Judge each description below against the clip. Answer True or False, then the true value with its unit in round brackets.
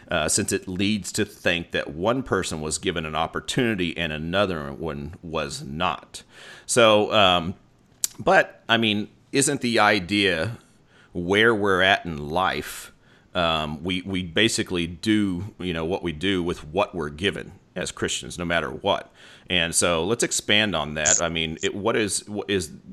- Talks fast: False (165 wpm)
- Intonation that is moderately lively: True (3.9 semitones)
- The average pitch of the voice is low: True (95 Hz)